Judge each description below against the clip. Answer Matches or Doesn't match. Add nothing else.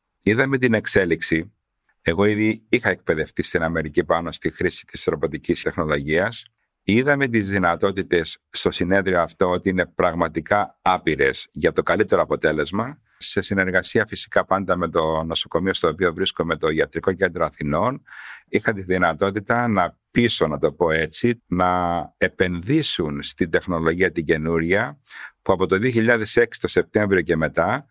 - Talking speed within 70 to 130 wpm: Doesn't match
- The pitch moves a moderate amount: Matches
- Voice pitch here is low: Matches